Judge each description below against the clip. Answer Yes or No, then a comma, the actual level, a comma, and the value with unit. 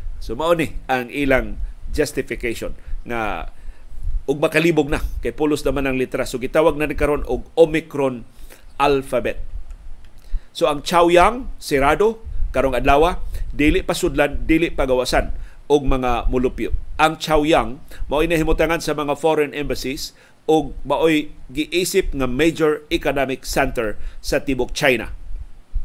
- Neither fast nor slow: Yes, average, 130 wpm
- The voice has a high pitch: No, medium, 140 Hz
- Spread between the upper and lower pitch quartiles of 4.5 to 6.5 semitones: No, average, 4.1 semitones